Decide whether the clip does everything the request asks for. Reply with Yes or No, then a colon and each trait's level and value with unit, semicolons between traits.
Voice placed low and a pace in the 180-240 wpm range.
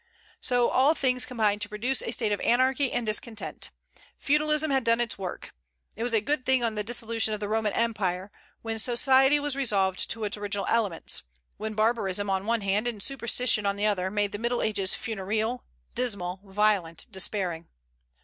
No: high, 220 Hz; average, 185 wpm